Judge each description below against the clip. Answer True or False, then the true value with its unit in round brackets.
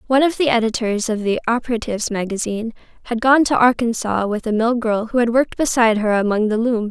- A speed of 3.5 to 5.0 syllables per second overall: False (6.3 syllables/s)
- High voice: True (230 Hz)